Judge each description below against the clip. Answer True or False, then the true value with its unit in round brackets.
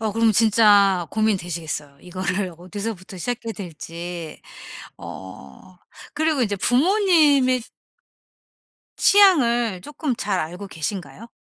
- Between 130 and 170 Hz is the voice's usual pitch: False (205 Hz)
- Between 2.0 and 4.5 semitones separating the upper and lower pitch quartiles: False (5.4 semitones)